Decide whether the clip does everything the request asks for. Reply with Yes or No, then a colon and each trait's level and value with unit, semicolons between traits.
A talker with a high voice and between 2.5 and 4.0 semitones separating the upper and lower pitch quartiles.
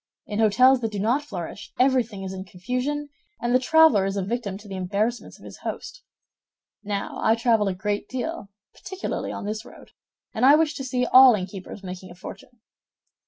No: high, 220 Hz; average, 4.5 semitones